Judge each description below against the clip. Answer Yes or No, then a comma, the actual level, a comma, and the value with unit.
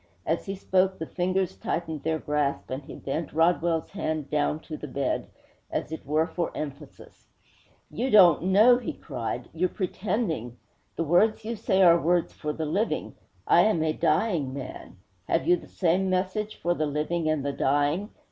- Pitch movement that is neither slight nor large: Yes, average, 3.8 semitones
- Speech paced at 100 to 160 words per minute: No, average, 175 wpm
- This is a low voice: No, medium, 165 Hz